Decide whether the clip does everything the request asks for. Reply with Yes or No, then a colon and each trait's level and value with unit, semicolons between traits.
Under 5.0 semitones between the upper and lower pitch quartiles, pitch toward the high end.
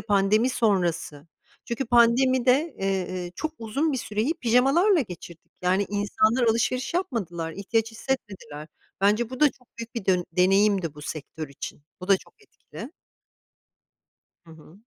No: wide, 5.6 semitones; high, 215 Hz